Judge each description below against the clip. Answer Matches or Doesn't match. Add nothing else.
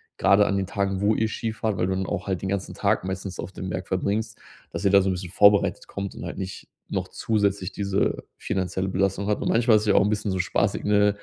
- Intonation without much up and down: Matches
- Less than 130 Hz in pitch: Matches